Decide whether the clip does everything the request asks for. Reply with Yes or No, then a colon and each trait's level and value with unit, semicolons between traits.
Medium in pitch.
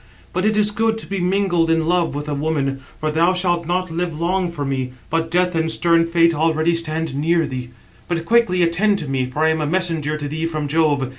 Yes: medium, 165 Hz